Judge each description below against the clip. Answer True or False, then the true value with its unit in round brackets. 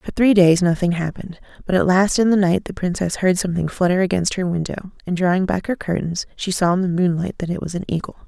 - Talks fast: True (245 wpm)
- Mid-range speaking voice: True (180 Hz)